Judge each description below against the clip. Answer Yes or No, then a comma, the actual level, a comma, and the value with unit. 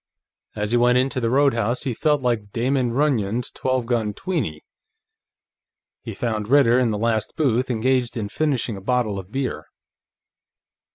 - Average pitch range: Yes, average, 3.0 semitones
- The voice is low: Yes, low, 120 Hz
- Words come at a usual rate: Yes, average, 155 wpm